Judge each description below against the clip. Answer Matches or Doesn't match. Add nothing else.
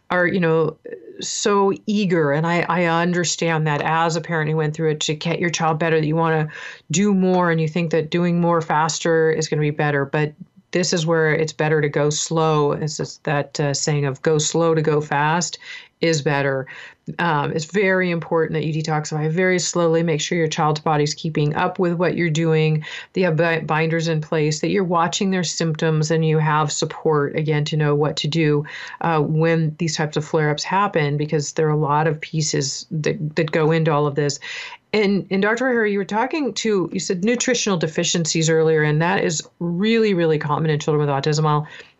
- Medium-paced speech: Doesn't match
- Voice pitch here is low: Doesn't match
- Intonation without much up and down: Matches